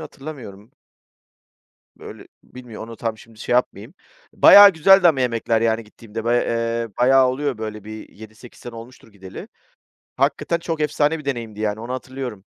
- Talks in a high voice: No, low, 120 Hz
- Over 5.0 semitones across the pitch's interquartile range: No, average, 3.7 semitones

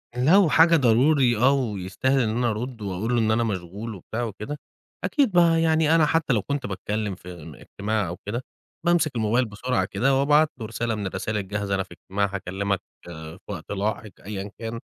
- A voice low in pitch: Yes, low, 110 Hz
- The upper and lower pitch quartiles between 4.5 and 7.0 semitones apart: Yes, average, 5.2 semitones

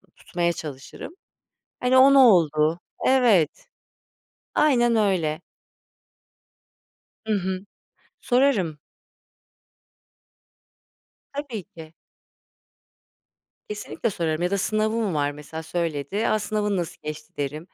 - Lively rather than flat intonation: Yes, wide, 6.0 semitones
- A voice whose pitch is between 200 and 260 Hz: No, medium, 185 Hz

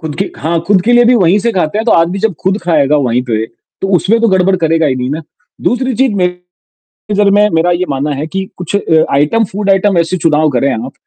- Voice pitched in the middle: Yes, medium, 180 Hz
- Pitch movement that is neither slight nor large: Yes, average, 4.9 semitones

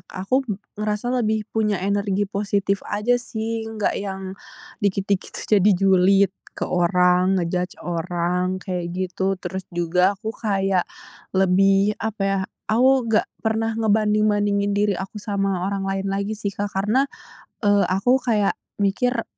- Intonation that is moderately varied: No, narrow, 2.0 semitones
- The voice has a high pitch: Yes, high, 200 Hz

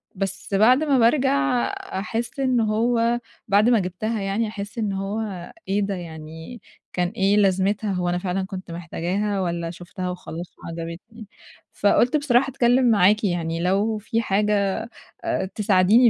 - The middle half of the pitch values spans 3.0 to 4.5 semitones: Yes, average, 4.0 semitones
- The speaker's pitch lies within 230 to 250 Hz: No, high, 200 Hz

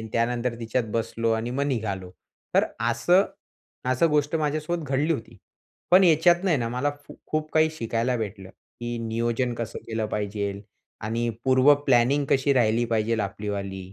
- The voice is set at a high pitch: No, low, 120 Hz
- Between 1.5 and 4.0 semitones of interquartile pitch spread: No, average, 4.6 semitones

